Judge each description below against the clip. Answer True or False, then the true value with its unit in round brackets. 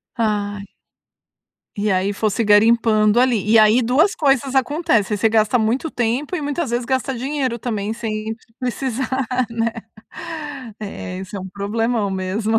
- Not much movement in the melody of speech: False (3.4 semitones)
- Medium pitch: False (225 Hz)